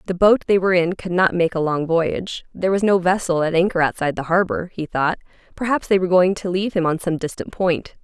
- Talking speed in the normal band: No, fast, 245 wpm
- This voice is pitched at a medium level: Yes, medium, 180 Hz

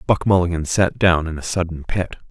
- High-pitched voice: No, very low, 85 Hz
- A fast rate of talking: Yes, fast, 210 wpm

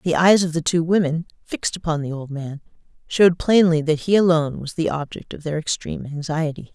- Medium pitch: Yes, medium, 160 Hz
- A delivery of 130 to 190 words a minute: No, fast, 205 wpm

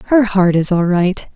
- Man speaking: No, female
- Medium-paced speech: No, fast, 220 wpm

